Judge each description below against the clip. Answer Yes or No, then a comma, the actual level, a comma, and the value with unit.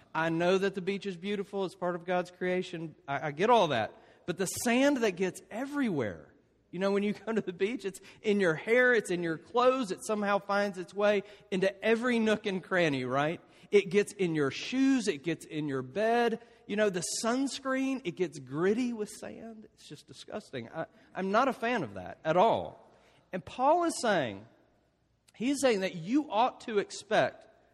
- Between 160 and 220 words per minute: Yes, average, 200 wpm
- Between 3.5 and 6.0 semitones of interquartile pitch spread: Yes, average, 4.3 semitones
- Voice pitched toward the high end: Yes, high, 200 Hz